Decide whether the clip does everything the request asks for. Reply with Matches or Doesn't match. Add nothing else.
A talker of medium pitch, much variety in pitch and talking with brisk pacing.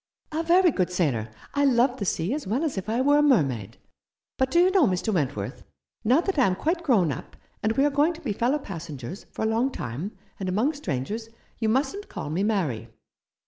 Doesn't match